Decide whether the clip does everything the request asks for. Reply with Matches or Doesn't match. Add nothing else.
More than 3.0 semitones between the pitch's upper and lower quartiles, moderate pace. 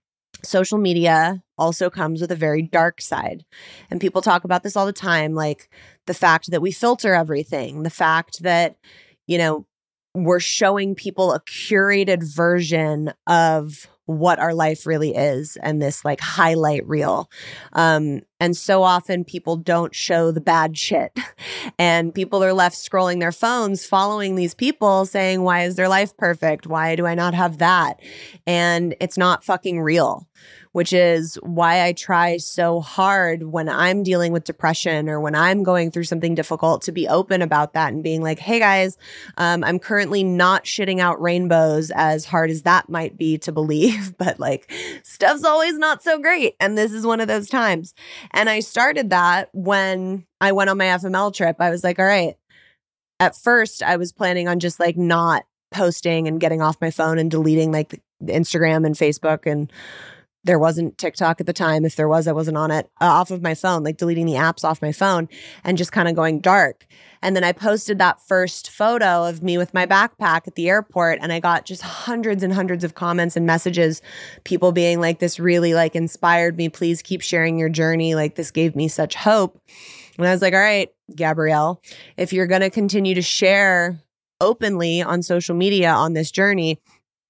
Doesn't match